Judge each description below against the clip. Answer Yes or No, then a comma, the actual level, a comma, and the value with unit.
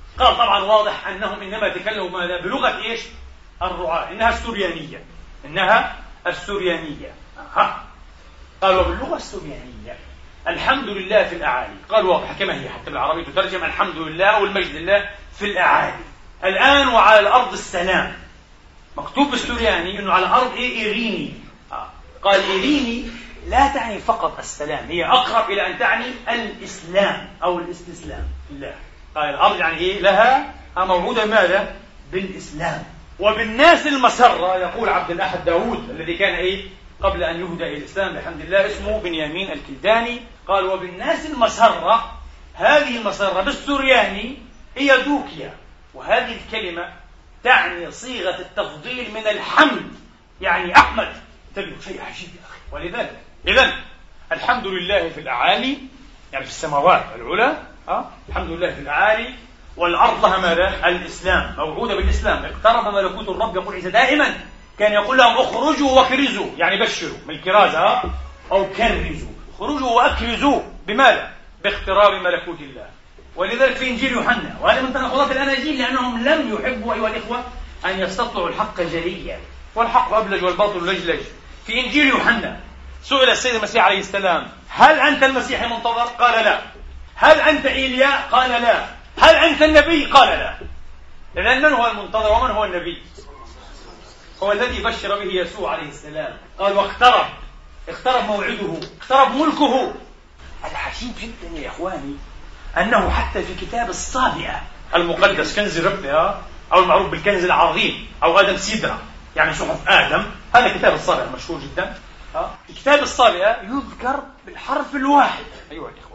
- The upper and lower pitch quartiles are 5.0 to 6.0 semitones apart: Yes, wide, 5.5 semitones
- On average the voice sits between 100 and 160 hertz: No, high, 215 Hz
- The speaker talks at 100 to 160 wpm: Yes, average, 130 wpm